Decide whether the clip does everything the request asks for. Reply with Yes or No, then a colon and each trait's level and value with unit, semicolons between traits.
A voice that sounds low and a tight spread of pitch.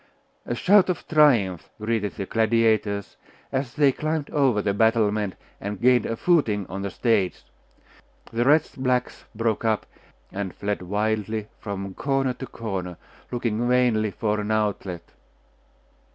No: low, 110 Hz; average, 3.6 semitones